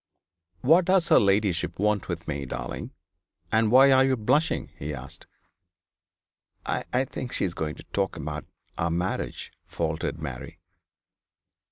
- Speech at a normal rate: Yes, average, 145 wpm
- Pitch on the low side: Yes, very low, 95 Hz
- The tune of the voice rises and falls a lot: Yes, wide, 8.6 semitones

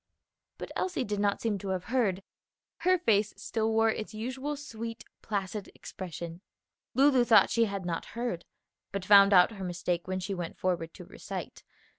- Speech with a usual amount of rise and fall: Yes, average, 3.6 semitones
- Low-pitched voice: No, high, 205 Hz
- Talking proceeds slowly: No, average, 170 wpm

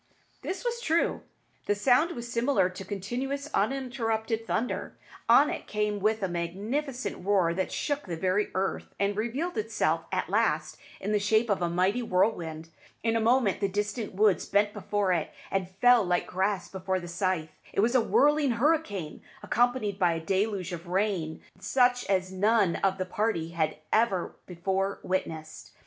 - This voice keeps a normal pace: Yes, average, 165 wpm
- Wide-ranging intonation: No, average, 4.0 semitones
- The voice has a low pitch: No, high, 205 Hz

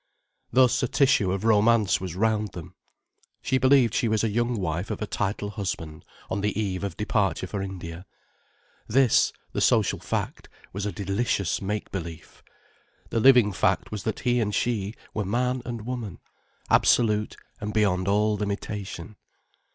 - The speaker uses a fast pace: No, average, 160 wpm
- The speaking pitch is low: Yes, low, 105 Hz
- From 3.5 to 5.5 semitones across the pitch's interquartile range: No, average, 3.0 semitones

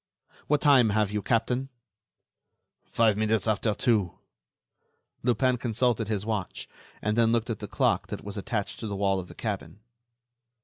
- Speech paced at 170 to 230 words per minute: No, average, 150 wpm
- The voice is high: No, low, 110 Hz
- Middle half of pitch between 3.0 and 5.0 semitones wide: No, narrow, 2.5 semitones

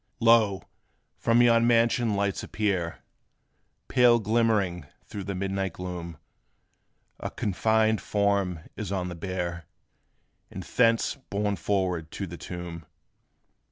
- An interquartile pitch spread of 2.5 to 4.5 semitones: Yes, average, 3.8 semitones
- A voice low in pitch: Yes, low, 100 Hz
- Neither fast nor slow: No, slow, 115 wpm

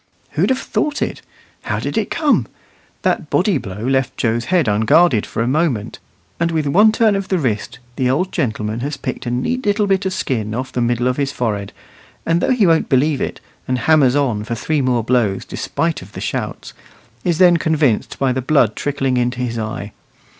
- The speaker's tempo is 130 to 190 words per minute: No, fast, 205 wpm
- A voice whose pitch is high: No, low, 135 Hz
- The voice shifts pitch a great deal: Yes, wide, 6.0 semitones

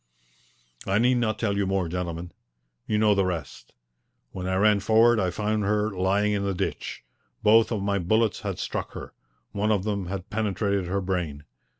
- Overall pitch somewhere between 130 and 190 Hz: No, low, 100 Hz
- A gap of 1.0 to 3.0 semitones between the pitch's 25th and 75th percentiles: Yes, narrow, 2.5 semitones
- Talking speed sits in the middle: Yes, average, 185 wpm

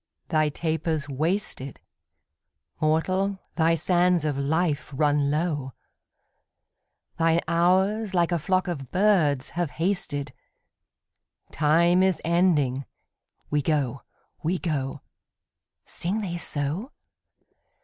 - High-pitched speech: No, medium, 165 Hz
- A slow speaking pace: Yes, slow, 100 wpm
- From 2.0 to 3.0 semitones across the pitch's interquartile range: No, average, 3.7 semitones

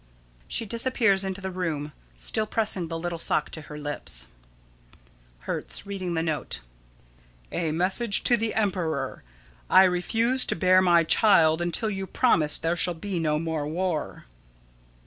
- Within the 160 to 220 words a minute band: No, average, 145 wpm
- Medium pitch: Yes, medium, 180 Hz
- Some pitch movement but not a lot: Yes, average, 3.8 semitones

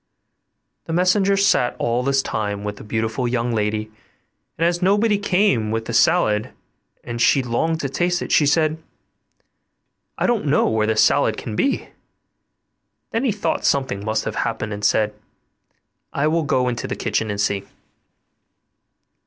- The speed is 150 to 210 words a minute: Yes, average, 160 wpm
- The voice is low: Yes, low, 125 Hz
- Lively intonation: Yes, wide, 7.9 semitones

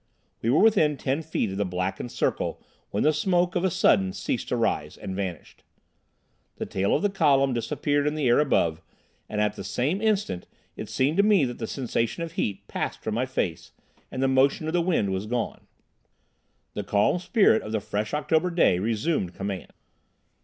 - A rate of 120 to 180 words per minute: No, average, 195 wpm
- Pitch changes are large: Yes, wide, 7.8 semitones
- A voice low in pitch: Yes, low, 130 Hz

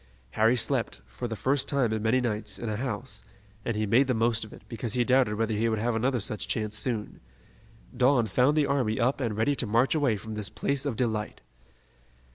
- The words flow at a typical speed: No, fast, 220 wpm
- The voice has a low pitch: Yes, low, 115 Hz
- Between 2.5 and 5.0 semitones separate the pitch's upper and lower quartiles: Yes, average, 3.0 semitones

